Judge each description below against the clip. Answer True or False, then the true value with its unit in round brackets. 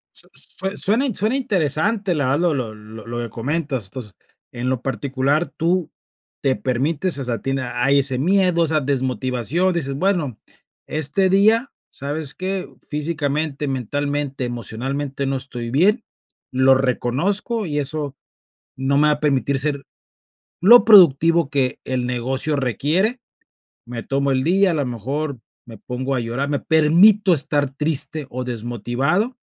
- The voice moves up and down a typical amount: True (4.6 semitones)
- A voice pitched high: False (140 Hz)